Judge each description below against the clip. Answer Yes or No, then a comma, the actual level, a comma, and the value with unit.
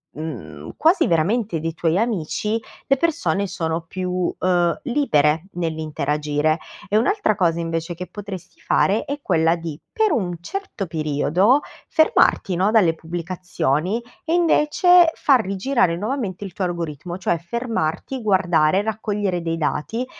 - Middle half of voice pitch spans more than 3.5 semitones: Yes, wide, 5.4 semitones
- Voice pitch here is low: No, medium, 180 Hz